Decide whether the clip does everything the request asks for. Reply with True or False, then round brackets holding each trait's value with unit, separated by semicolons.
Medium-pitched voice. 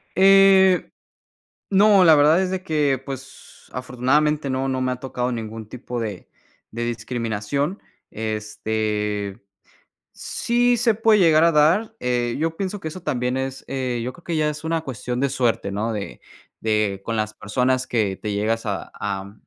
False (130 Hz)